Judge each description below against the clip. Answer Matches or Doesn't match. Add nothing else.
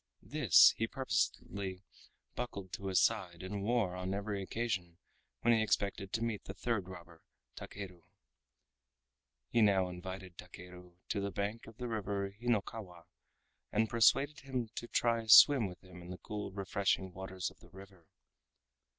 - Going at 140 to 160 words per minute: Matches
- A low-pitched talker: Matches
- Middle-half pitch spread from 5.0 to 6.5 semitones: Doesn't match